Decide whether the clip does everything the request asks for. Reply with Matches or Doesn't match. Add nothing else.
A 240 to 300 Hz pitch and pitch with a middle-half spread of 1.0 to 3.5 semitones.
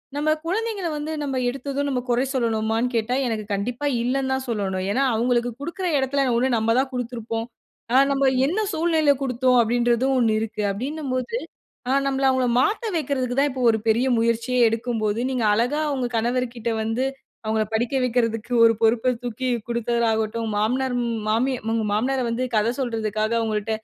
Matches